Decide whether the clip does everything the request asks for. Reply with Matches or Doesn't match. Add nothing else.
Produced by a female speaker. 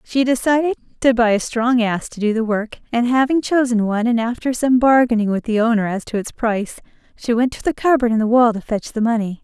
Matches